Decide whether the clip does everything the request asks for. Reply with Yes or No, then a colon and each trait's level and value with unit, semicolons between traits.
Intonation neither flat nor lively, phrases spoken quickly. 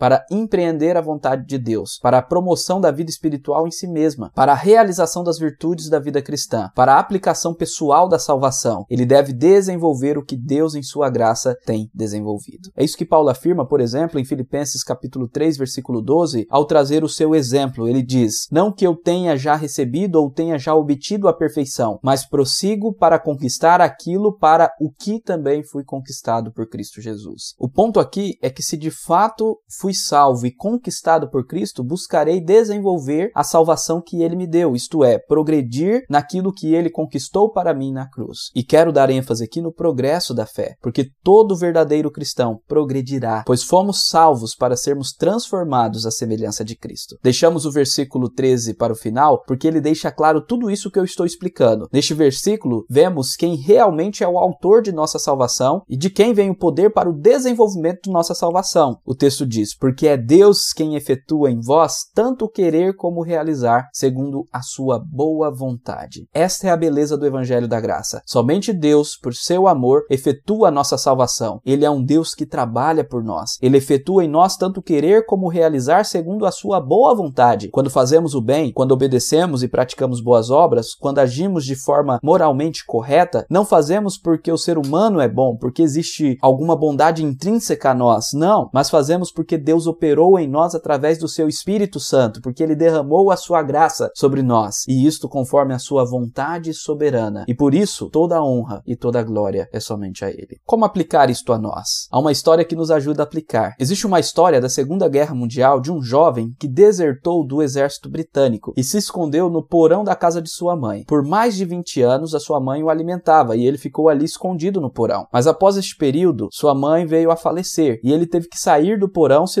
Yes: average, 4.5 semitones; fast, 195 wpm